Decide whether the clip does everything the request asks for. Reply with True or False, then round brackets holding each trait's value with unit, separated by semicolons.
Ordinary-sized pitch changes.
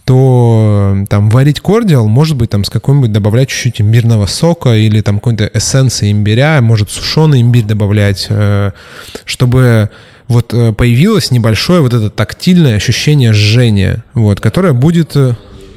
True (3.8 semitones)